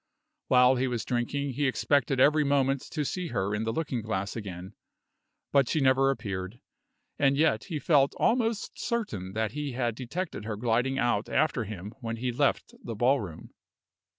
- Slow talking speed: No, average, 170 wpm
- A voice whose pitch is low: Yes, low, 125 Hz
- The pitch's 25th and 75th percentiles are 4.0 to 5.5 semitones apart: Yes, average, 4.3 semitones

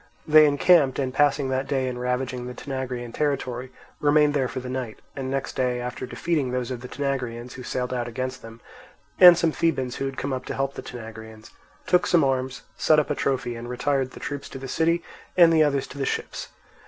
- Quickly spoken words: Yes, fast, 215 wpm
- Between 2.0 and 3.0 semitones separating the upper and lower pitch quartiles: Yes, narrow, 2.4 semitones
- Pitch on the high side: No, low, 130 Hz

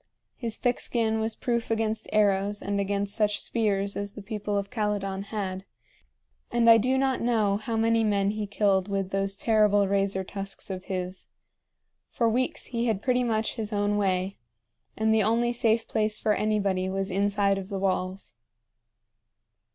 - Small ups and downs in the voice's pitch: Yes, narrow, 2.2 semitones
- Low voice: No, high, 205 Hz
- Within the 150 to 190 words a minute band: Yes, average, 165 wpm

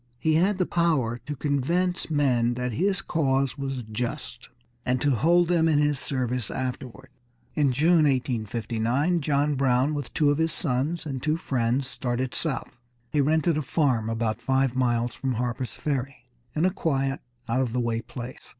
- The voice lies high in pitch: No, low, 135 Hz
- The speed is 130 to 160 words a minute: No, average, 170 wpm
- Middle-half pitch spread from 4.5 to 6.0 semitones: No, average, 3.8 semitones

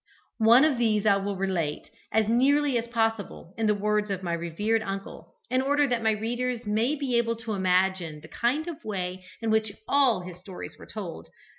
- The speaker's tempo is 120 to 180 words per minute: No, average, 195 wpm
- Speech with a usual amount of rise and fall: Yes, average, 3.9 semitones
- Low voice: No, high, 220 Hz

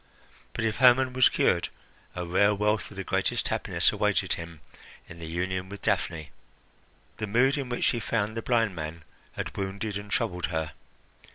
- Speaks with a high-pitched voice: No, low, 100 Hz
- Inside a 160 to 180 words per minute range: Yes, average, 175 wpm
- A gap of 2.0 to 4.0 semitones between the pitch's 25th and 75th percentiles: No, average, 4.5 semitones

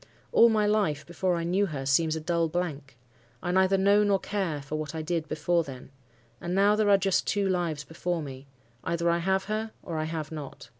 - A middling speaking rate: No, fast, 215 wpm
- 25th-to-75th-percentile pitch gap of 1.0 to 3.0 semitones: No, average, 3.9 semitones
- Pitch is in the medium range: Yes, medium, 170 Hz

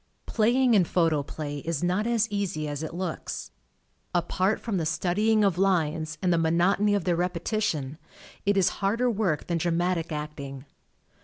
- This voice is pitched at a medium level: Yes, medium, 175 Hz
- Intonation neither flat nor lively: Yes, average, 4.3 semitones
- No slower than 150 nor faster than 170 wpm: Yes, average, 155 wpm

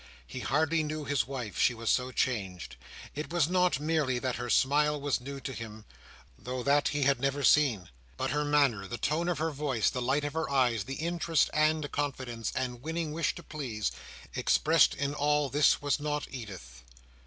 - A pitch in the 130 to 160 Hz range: Yes, medium, 140 Hz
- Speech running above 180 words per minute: Yes, average, 190 wpm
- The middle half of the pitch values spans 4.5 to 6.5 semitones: No, average, 3.5 semitones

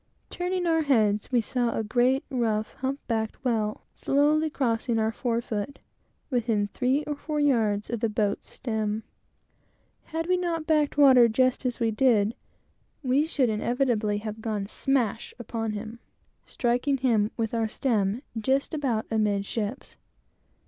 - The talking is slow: No, average, 145 wpm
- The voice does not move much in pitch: No, average, 3.8 semitones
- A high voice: Yes, high, 235 Hz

